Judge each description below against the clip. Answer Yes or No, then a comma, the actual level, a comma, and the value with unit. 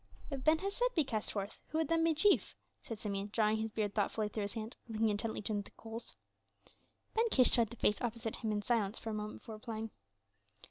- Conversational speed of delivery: No, fast, 225 wpm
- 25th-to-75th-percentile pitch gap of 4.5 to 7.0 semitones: No, average, 3.2 semitones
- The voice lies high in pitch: Yes, high, 225 Hz